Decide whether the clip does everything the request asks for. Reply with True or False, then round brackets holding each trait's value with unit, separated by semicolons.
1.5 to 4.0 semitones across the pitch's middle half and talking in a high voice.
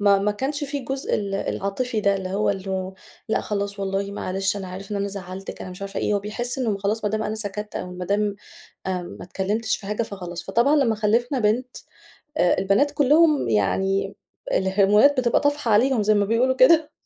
True (3.7 semitones; 205 Hz)